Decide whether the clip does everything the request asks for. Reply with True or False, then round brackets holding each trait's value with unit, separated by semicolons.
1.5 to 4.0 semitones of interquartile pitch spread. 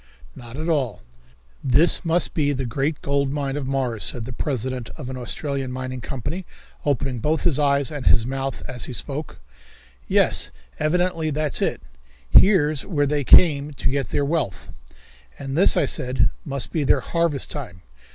True (2.8 semitones)